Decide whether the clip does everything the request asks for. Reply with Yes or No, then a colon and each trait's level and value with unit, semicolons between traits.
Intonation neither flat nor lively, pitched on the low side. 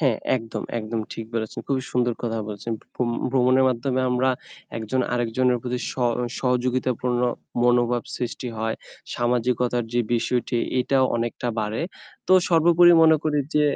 No: narrow, 1.7 semitones; low, 125 Hz